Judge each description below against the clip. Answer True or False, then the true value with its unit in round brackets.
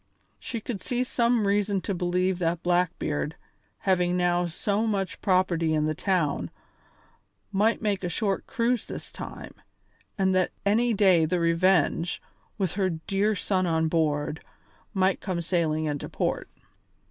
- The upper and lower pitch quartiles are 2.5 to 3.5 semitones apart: True (3.2 semitones)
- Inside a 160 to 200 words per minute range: False (145 wpm)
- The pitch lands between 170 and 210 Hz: True (185 Hz)